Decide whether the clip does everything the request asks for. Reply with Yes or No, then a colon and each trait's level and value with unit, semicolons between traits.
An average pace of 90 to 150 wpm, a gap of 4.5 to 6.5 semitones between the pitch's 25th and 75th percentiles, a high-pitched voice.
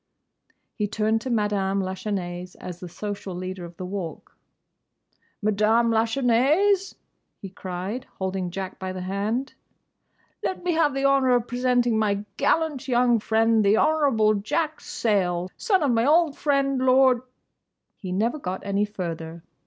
Yes: average, 145 wpm; wide, 5.4 semitones; high, 220 Hz